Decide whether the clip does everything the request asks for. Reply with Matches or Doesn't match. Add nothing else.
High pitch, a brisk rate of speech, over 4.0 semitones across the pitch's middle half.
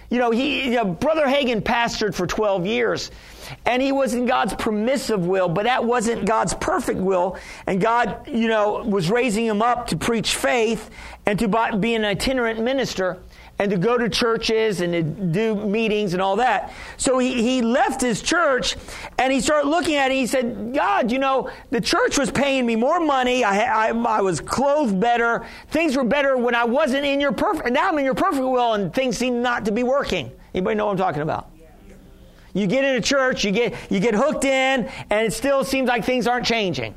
Doesn't match